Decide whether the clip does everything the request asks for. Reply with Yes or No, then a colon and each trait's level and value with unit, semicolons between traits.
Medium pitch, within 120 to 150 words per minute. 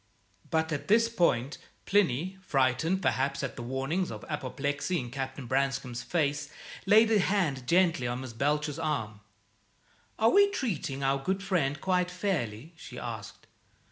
Yes: medium, 145 Hz; average, 145 wpm